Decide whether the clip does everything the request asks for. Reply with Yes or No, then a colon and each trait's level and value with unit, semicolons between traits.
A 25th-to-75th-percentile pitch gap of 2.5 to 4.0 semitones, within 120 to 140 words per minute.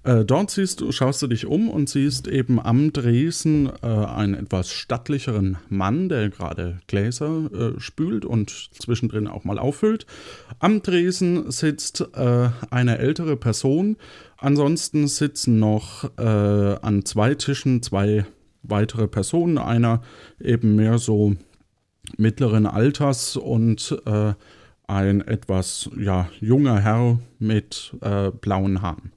No: average, 5.2 semitones; average, 130 wpm